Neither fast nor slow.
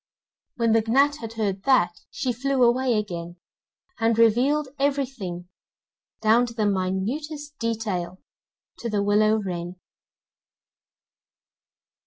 No: slow, 110 wpm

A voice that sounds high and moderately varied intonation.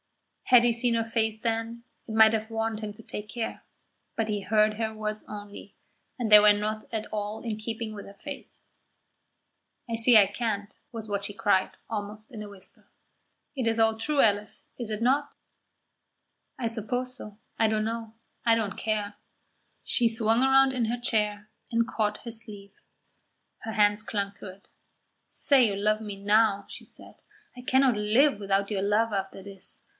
No: high, 220 Hz; narrow, 1.8 semitones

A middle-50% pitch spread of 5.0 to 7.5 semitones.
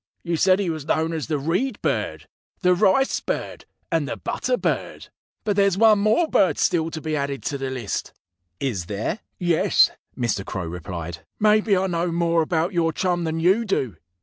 Yes: wide, 5.5 semitones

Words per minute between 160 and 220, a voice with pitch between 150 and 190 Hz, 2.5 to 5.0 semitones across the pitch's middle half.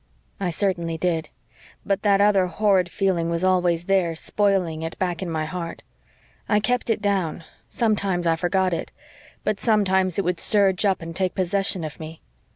Yes: average, 170 wpm; medium, 185 Hz; average, 2.9 semitones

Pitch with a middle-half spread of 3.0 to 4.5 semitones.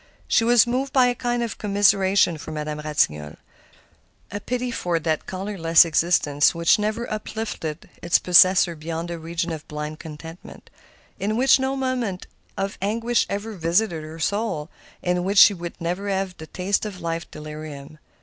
No: average, 4.9 semitones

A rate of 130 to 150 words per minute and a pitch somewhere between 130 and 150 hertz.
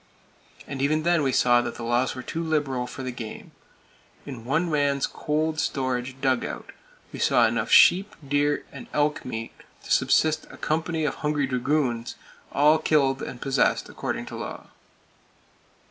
No: average, 160 wpm; medium, 140 Hz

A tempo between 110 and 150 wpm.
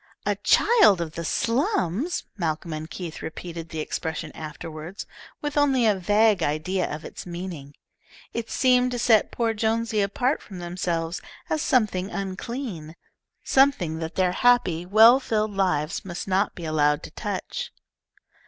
Yes: average, 145 wpm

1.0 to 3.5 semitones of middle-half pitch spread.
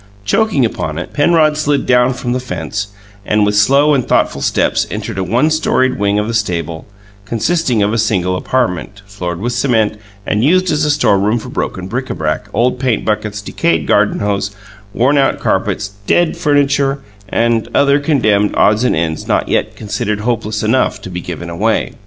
No: average, 4.8 semitones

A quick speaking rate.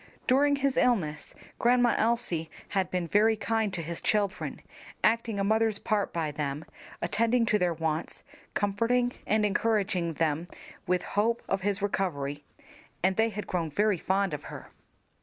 No: average, 155 wpm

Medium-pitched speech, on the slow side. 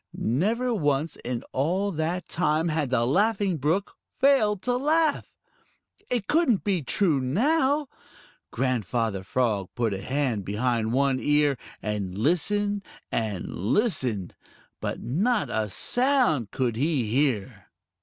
Yes: medium, 150 Hz; slow, 125 wpm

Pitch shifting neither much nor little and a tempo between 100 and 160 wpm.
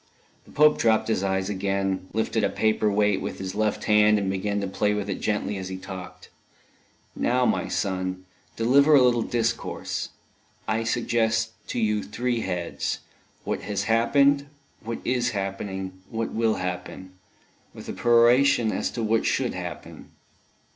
Yes: average, 3.3 semitones; average, 155 wpm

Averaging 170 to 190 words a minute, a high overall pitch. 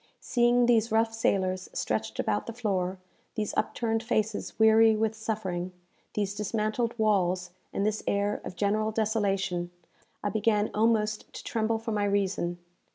No: average, 145 wpm; high, 215 Hz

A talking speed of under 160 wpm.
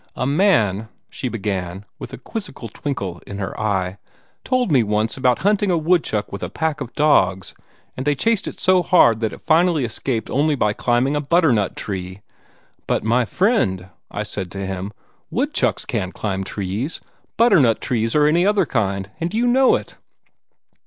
No: average, 175 wpm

